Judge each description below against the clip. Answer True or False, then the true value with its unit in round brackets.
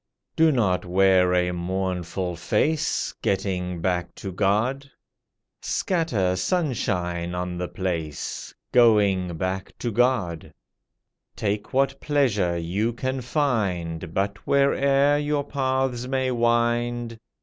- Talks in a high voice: False (105 Hz)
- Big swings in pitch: True (6.4 semitones)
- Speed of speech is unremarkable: False (105 wpm)